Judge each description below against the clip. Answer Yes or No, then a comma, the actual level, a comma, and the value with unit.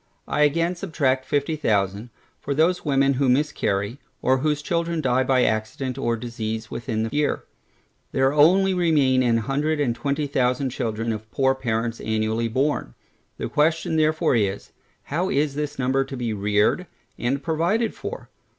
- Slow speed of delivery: No, average, 155 wpm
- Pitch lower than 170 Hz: Yes, low, 135 Hz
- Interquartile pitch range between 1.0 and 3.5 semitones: No, average, 4.5 semitones